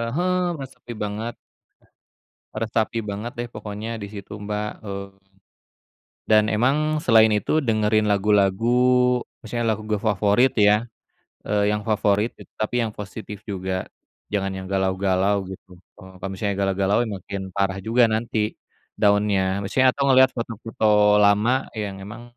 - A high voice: No, low, 105 Hz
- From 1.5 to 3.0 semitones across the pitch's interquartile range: Yes, average, 2.7 semitones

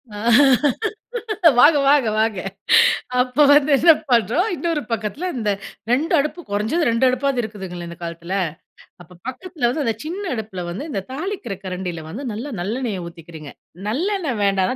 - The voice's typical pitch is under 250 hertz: Yes, high, 230 Hz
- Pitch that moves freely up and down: Yes, wide, 7.5 semitones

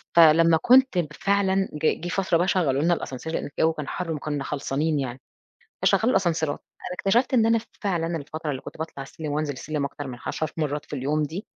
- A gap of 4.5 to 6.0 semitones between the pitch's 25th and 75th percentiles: No, average, 3.7 semitones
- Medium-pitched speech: Yes, medium, 160 Hz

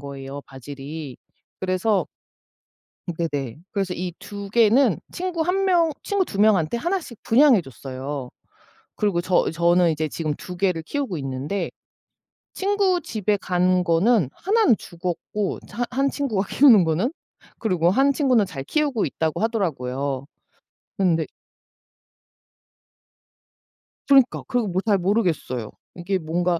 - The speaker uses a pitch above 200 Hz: No, medium, 185 Hz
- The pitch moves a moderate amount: No, wide, 6.9 semitones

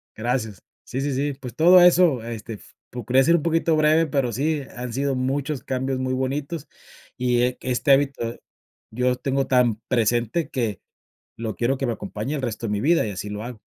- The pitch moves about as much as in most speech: Yes, average, 3.2 semitones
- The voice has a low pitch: Yes, low, 130 Hz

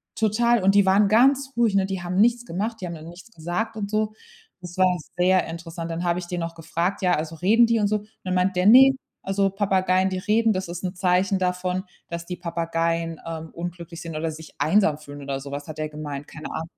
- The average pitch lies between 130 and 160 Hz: No, medium, 180 Hz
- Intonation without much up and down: No, average, 3.4 semitones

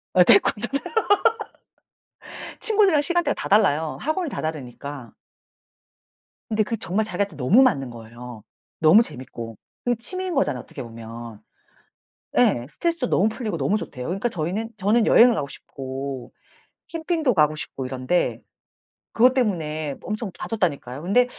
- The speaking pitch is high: No, medium, 180 Hz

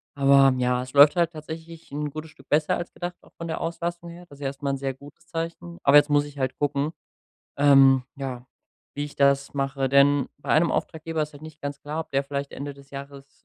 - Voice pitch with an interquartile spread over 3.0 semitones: No, narrow, 2.5 semitones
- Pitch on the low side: No, medium, 145 Hz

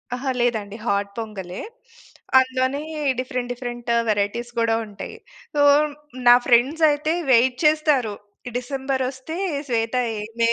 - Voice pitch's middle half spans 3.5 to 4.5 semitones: No, average, 2.7 semitones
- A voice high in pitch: Yes, high, 245 Hz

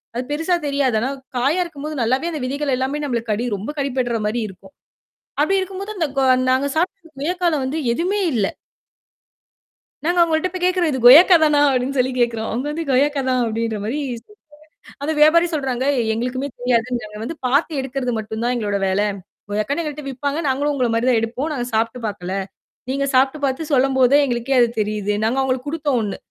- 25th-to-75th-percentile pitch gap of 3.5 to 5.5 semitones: Yes, average, 4.1 semitones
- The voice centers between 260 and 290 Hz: Yes, very high, 265 Hz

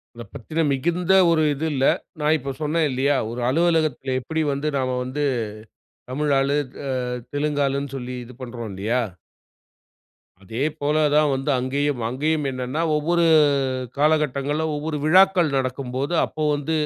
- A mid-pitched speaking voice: Yes, medium, 145 Hz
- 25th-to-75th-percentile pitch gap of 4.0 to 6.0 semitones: No, average, 3.1 semitones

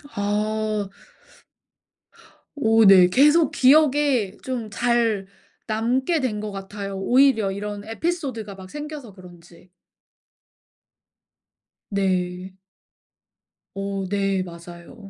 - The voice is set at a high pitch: Yes, high, 210 Hz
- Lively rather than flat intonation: No, average, 4.6 semitones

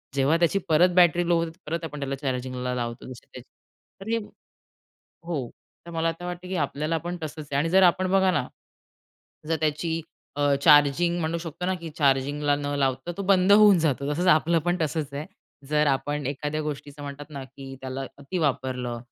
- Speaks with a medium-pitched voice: Yes, medium, 150 Hz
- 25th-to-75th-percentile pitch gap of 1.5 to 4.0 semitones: Yes, average, 3.7 semitones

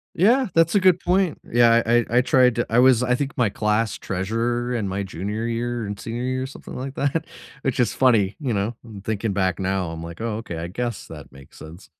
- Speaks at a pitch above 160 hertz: No, low, 115 Hz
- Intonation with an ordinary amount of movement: Yes, average, 4.2 semitones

